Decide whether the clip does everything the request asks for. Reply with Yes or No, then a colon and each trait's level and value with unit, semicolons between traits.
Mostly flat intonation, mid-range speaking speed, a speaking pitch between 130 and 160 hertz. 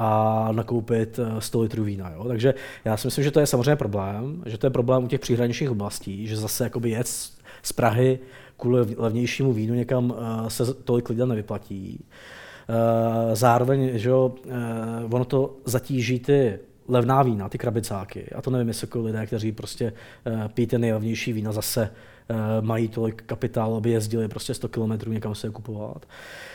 No: narrow, 2.3 semitones; average, 160 wpm; low, 115 Hz